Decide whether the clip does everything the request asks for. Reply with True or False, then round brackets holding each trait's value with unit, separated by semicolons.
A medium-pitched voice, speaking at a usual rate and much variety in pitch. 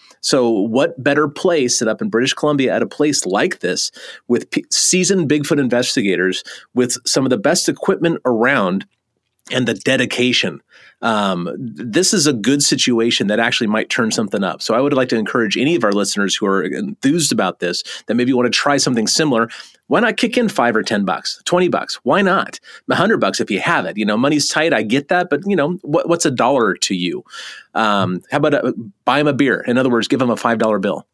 False (145 Hz; 220 wpm; 6.1 semitones)